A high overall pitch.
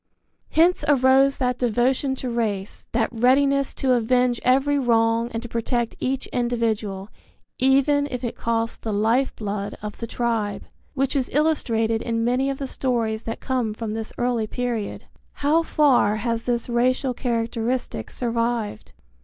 Yes: high, 240 Hz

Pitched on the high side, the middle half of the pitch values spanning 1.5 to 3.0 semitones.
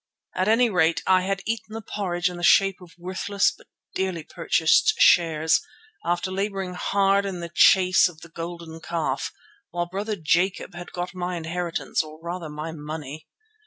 No: medium, 175 Hz; average, 2.7 semitones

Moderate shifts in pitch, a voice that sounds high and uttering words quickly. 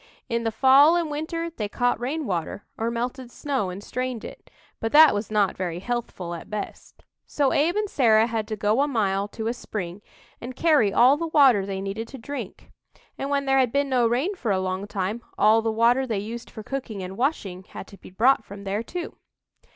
Yes: average, 5.0 semitones; high, 230 Hz; fast, 215 wpm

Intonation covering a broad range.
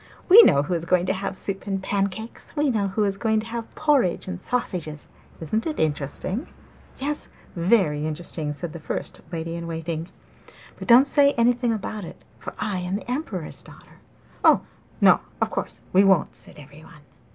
Yes: wide, 5.9 semitones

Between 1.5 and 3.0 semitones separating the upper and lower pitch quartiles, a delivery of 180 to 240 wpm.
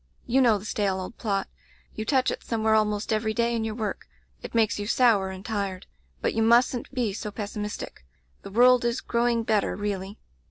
Yes: narrow, 2.4 semitones; average, 200 wpm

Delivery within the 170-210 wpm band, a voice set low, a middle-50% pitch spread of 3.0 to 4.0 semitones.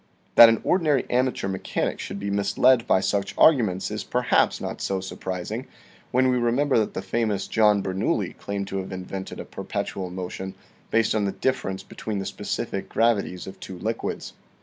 Yes: average, 180 wpm; low, 100 Hz; average, 3.7 semitones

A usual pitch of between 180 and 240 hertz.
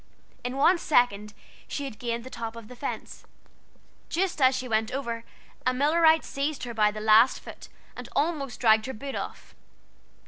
No: very high, 250 Hz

